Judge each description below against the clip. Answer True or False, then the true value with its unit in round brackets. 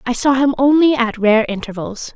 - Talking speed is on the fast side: False (195 wpm)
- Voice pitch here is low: False (245 Hz)